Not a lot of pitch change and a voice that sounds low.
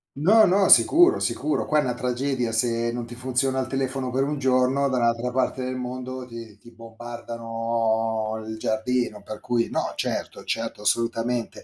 Yes: narrow, 2.2 semitones; low, 125 Hz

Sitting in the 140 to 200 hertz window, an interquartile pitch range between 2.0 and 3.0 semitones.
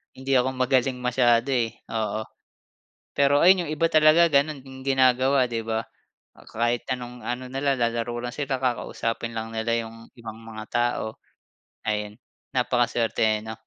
No: low, 120 Hz; average, 2.7 semitones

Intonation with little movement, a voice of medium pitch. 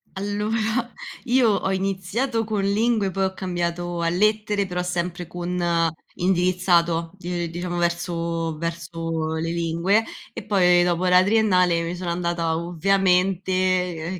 Yes: narrow, 2.3 semitones; medium, 180 Hz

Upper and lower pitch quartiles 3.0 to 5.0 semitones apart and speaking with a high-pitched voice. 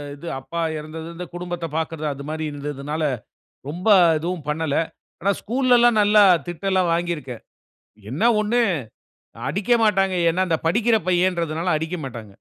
No: average, 3.8 semitones; medium, 170 Hz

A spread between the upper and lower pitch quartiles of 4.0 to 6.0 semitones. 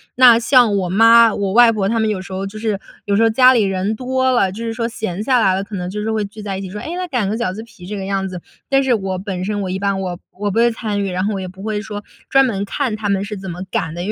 No: average, 2.9 semitones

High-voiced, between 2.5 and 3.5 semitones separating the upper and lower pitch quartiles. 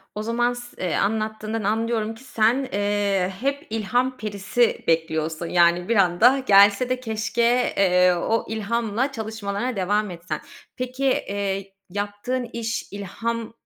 Yes: high, 215 Hz; average, 3.2 semitones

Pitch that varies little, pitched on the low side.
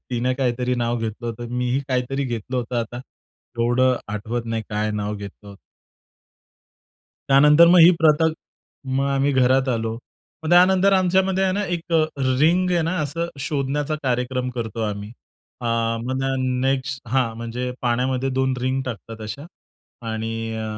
No: average, 3.3 semitones; low, 125 Hz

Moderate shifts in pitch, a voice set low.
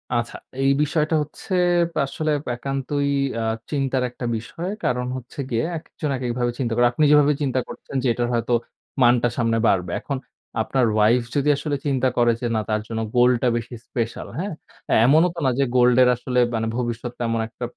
Yes: average, 3.0 semitones; low, 125 Hz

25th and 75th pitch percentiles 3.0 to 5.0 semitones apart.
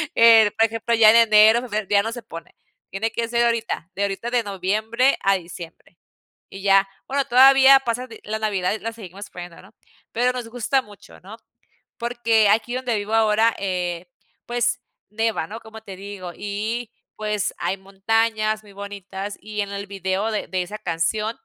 No: narrow, 2.6 semitones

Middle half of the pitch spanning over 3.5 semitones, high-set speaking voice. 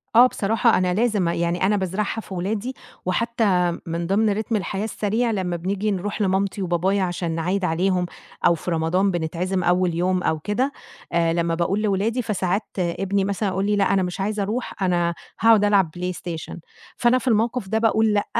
No: average, 3.1 semitones; high, 195 Hz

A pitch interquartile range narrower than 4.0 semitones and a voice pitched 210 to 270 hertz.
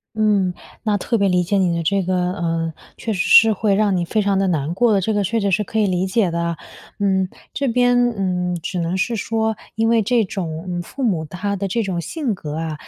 No: average, 3.6 semitones; high, 195 Hz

